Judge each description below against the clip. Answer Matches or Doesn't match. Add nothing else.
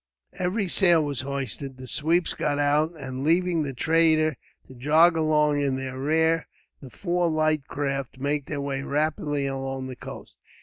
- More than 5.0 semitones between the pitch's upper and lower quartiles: Doesn't match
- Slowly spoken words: Doesn't match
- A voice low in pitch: Doesn't match